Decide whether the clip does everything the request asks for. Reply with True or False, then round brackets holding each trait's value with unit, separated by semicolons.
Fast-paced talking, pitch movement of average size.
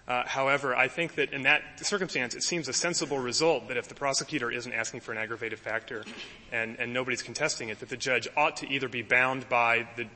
True (235 wpm; 3.8 semitones)